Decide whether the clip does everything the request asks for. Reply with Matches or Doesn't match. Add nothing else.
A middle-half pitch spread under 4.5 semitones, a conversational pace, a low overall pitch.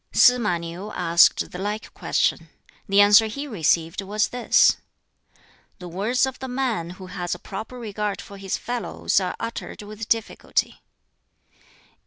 Doesn't match